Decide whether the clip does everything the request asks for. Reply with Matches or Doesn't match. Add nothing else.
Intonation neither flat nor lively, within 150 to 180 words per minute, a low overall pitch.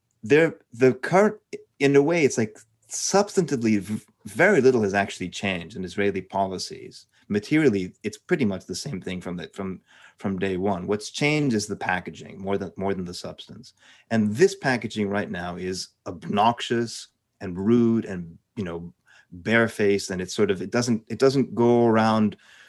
Matches